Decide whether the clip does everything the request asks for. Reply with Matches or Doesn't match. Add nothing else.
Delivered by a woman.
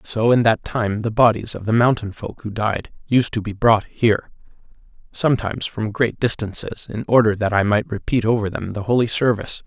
Doesn't match